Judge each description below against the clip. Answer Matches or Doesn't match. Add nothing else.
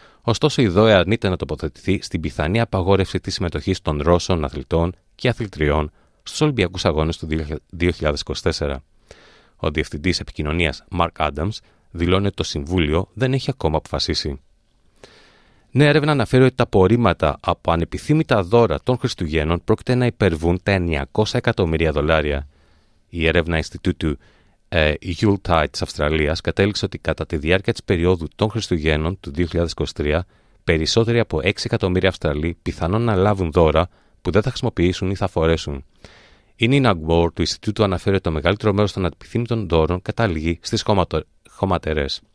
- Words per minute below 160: Matches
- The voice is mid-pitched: Doesn't match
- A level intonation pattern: Doesn't match